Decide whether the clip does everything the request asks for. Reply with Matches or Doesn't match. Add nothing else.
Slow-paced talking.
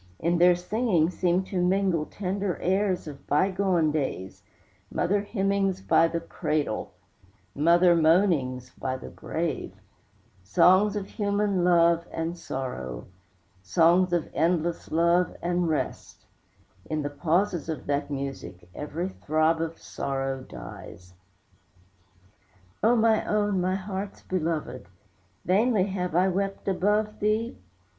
Matches